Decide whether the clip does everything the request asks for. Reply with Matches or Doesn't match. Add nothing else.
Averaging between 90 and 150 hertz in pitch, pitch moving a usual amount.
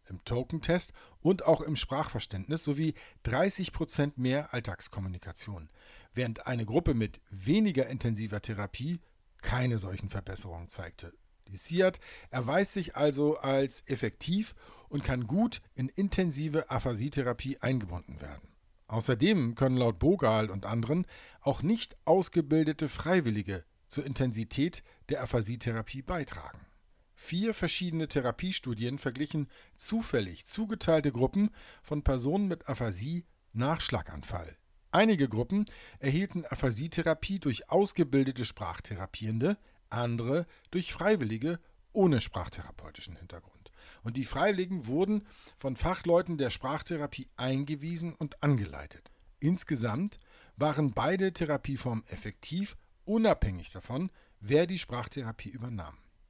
Doesn't match